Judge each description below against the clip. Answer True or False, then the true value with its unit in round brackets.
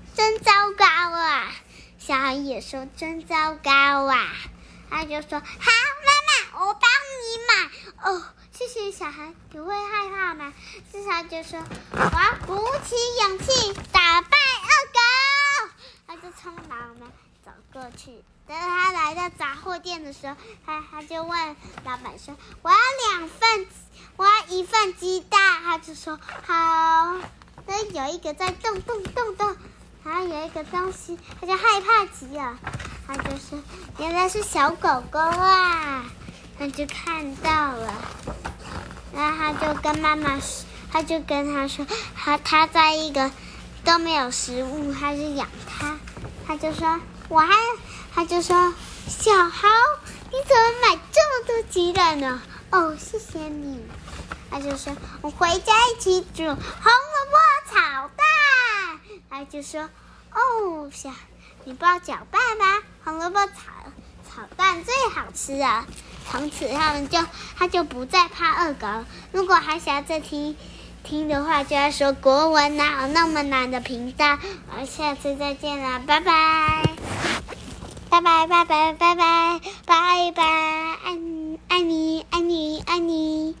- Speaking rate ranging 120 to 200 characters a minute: True (195 characters per minute)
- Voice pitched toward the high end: True (325 Hz)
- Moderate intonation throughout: True (4.1 semitones)